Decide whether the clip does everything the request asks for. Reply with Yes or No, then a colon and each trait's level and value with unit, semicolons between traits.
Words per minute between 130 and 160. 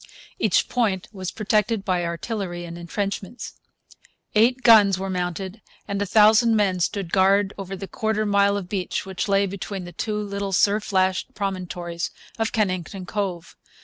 Yes: average, 155 wpm